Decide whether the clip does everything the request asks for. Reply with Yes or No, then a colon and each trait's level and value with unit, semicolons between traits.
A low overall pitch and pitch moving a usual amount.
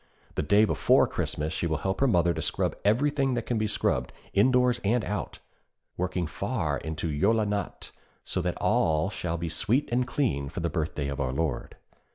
No: very low, 95 Hz; wide, 6.4 semitones